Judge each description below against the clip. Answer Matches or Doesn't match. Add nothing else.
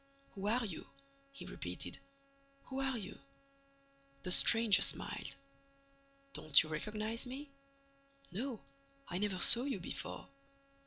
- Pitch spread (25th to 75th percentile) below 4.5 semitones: Doesn't match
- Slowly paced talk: Matches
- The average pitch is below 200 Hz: Doesn't match